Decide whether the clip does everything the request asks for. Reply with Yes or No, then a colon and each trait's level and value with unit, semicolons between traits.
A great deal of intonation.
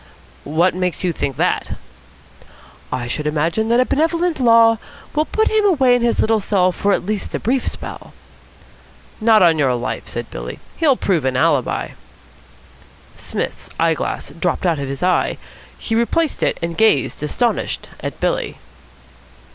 Yes: wide, 7.3 semitones